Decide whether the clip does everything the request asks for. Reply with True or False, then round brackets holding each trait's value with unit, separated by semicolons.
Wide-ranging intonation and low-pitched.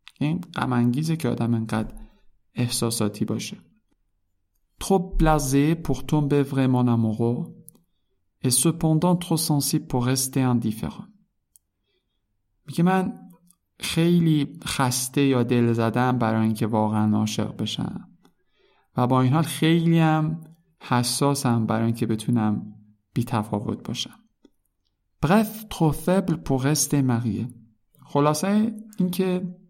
True (6.4 semitones; 130 Hz)